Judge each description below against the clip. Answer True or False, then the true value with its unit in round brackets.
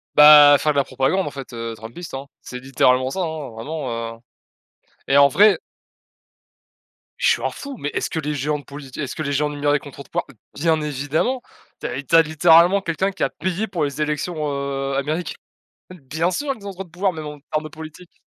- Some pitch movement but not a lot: True (3.7 semitones)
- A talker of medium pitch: True (150 Hz)